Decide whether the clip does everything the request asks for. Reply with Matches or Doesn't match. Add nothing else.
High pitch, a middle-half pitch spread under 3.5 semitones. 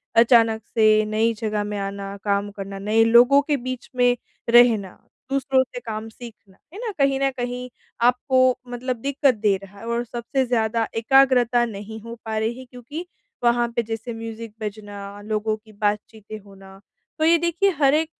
Matches